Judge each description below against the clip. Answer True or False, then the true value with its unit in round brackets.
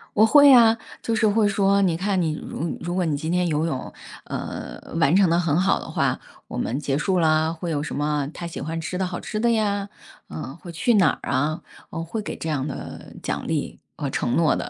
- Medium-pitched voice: True (170 Hz)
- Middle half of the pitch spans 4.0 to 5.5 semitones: True (4.4 semitones)